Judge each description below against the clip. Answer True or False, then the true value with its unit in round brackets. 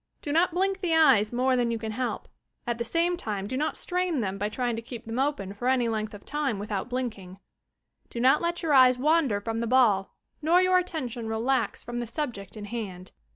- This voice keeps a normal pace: False (220 wpm)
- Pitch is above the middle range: True (245 Hz)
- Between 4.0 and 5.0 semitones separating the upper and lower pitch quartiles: False (5.5 semitones)